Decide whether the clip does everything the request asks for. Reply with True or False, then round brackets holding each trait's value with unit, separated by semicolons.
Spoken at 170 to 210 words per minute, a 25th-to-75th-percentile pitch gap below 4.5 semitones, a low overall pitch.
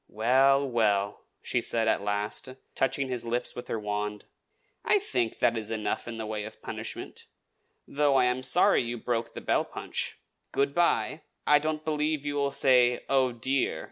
True (175 wpm; 3.6 semitones; 125 Hz)